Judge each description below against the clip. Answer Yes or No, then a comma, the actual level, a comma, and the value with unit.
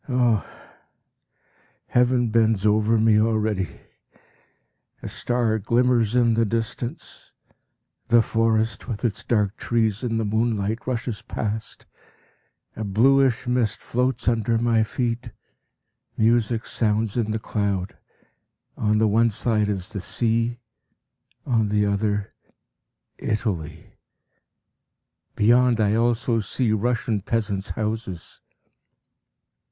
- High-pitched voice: No, low, 110 Hz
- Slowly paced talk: Yes, slow, 110 wpm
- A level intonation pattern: Yes, narrow, 2.0 semitones